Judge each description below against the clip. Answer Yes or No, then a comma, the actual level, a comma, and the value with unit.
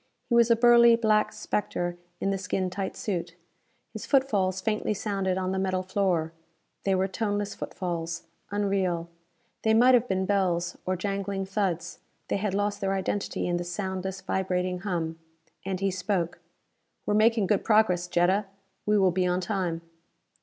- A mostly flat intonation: Yes, narrow, 2.3 semitones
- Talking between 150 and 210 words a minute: Yes, average, 165 wpm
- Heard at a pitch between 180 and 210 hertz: Yes, high, 190 Hz